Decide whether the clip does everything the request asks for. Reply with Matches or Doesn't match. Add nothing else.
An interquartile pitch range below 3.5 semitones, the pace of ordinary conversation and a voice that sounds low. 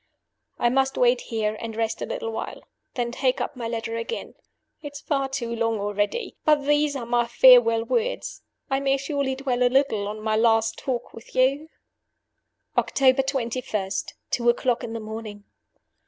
Doesn't match